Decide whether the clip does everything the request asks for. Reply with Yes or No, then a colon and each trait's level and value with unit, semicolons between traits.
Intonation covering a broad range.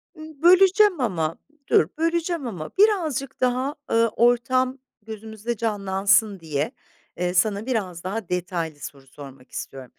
Yes: wide, 7.3 semitones